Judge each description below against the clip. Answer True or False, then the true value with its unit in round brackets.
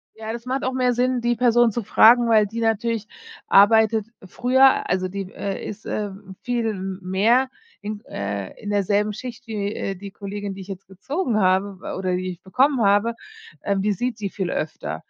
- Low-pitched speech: False (210 Hz)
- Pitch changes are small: False (3.4 semitones)